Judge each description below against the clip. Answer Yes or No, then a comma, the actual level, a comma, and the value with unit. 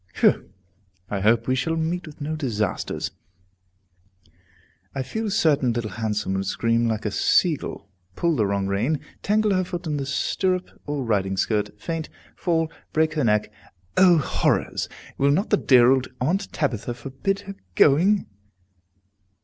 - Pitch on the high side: No, medium, 140 Hz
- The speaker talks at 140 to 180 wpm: Yes, average, 155 wpm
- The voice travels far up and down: Yes, wide, 7.0 semitones